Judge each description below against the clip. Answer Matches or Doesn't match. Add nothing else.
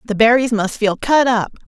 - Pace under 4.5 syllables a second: Doesn't match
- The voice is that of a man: Doesn't match